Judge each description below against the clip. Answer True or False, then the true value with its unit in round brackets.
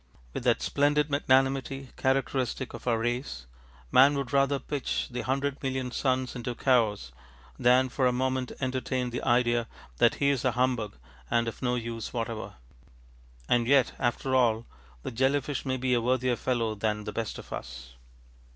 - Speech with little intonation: True (2.2 semitones)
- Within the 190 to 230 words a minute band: False (170 wpm)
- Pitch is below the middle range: True (125 Hz)